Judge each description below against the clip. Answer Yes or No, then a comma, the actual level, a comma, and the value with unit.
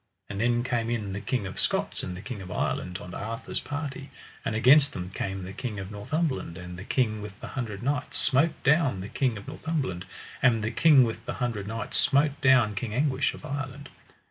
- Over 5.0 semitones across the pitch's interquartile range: Yes, wide, 5.5 semitones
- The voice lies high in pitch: No, low, 120 Hz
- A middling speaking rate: No, fast, 210 wpm